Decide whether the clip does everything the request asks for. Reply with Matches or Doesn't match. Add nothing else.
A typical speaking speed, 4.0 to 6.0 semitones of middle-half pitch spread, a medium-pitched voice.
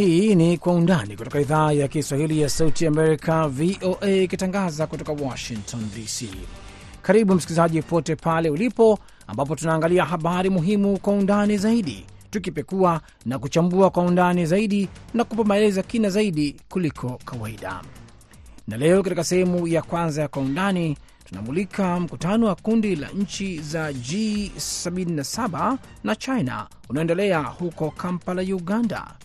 Matches